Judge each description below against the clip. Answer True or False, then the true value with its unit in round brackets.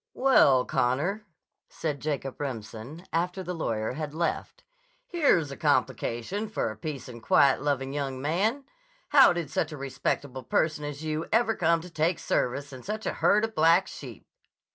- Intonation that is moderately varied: True (5.0 semitones)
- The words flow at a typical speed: True (165 wpm)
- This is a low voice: False (155 Hz)